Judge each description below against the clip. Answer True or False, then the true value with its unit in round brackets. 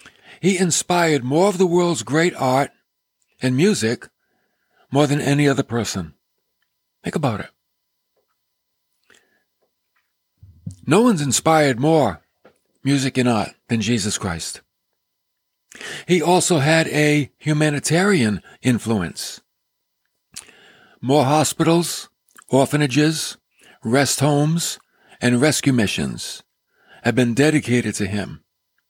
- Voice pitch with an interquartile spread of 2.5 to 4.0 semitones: False (4.9 semitones)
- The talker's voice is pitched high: False (140 Hz)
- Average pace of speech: False (100 wpm)